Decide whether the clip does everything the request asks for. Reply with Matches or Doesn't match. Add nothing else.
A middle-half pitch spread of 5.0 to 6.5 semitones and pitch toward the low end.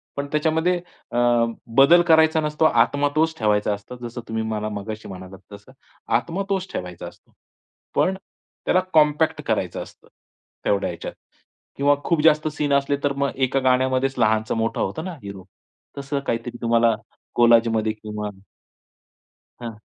Matches